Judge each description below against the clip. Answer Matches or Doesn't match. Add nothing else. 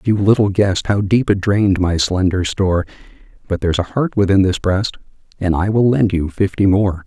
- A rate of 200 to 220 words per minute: Matches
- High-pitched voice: Doesn't match